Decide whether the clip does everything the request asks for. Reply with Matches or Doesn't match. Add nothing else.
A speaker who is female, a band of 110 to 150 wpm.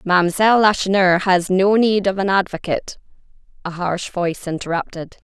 Matches